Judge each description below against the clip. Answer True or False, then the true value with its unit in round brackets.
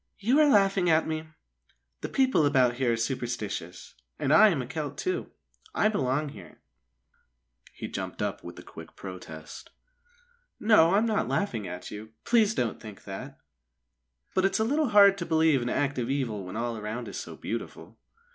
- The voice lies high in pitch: False (140 Hz)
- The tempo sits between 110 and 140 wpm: False (175 wpm)